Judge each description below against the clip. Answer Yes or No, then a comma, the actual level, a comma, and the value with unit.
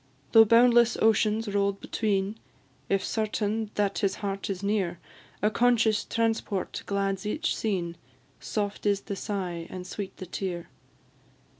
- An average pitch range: No, narrow, 2.2 semitones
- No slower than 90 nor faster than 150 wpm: Yes, slow, 135 wpm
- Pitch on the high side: Yes, high, 205 Hz